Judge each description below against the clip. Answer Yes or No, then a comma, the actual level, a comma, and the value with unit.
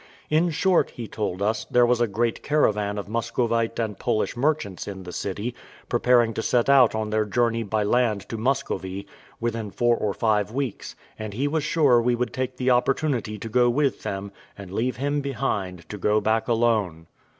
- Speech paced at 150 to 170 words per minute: No, average, 190 wpm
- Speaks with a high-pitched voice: No, low, 115 Hz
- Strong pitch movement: No, average, 3.1 semitones